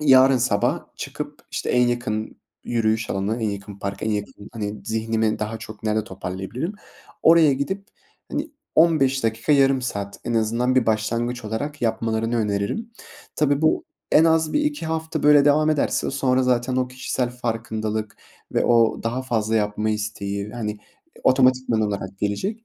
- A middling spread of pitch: Yes, average, 3.8 semitones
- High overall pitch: No, low, 115 Hz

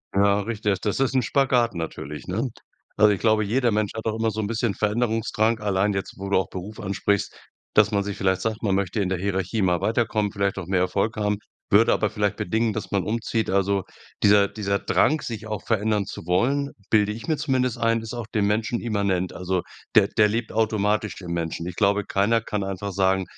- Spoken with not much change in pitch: Yes, narrow, 2.3 semitones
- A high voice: No, low, 105 Hz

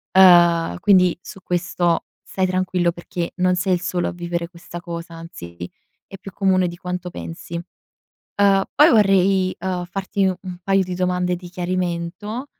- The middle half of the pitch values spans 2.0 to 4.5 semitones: No, narrow, 1.5 semitones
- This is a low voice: No, medium, 180 Hz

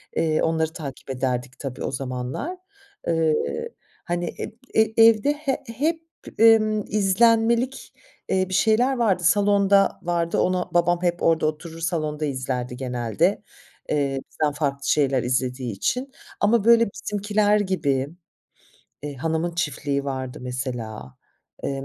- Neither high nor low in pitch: Yes, medium, 165 Hz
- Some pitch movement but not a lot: No, wide, 7.3 semitones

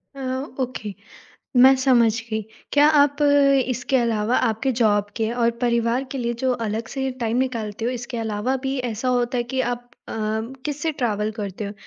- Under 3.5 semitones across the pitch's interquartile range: Yes, average, 2.9 semitones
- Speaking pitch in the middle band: No, high, 240 Hz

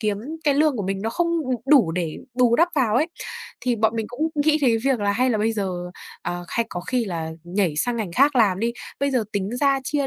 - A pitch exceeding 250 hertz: No, high, 230 Hz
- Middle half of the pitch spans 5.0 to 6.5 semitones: Yes, average, 5.3 semitones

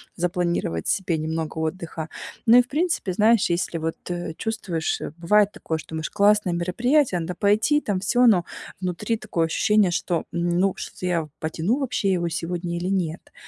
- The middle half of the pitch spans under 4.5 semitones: Yes, average, 3.9 semitones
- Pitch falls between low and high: Yes, medium, 180 Hz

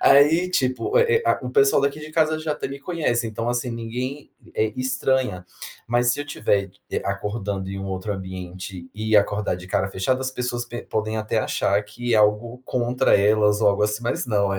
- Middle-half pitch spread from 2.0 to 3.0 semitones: No, average, 4.3 semitones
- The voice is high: No, low, 115 Hz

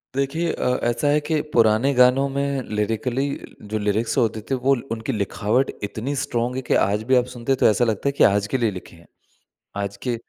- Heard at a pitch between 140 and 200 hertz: No, low, 120 Hz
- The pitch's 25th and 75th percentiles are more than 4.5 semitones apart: No, average, 3.9 semitones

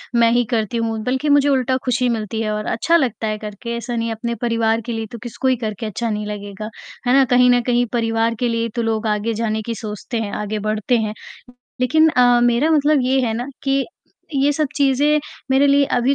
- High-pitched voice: Yes, high, 235 Hz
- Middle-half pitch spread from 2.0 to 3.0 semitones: Yes, average, 2.7 semitones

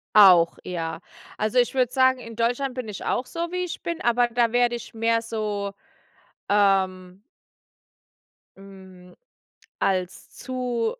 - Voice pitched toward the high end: Yes, high, 225 Hz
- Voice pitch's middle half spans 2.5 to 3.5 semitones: No, average, 4.2 semitones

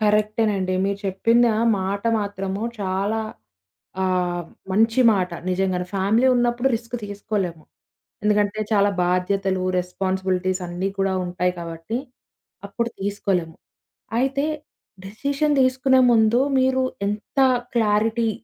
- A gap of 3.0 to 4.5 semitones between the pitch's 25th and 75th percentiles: Yes, average, 3.4 semitones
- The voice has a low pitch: No, high, 205 Hz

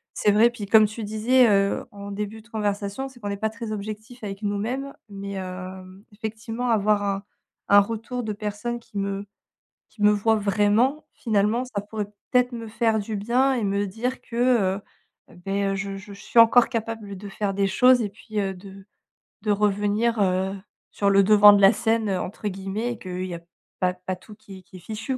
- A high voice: Yes, high, 210 Hz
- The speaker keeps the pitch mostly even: Yes, narrow, 2.2 semitones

